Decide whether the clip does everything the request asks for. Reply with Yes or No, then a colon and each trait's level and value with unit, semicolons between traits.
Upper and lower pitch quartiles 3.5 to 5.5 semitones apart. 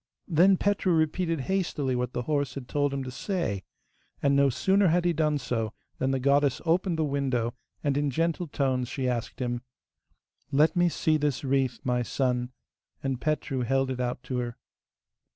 Yes: average, 4.0 semitones